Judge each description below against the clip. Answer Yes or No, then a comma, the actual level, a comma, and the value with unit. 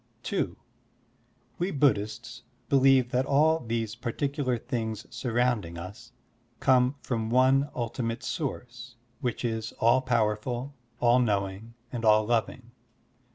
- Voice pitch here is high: No, low, 120 Hz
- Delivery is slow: Yes, slow, 115 wpm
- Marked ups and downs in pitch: No, narrow, 2.6 semitones